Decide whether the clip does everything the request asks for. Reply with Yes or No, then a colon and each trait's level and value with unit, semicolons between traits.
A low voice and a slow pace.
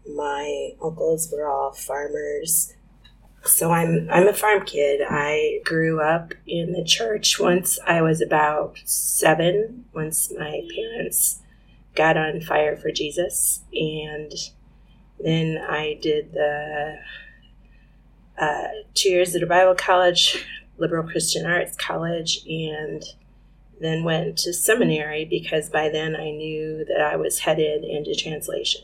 No: medium, 160 Hz; slow, 130 wpm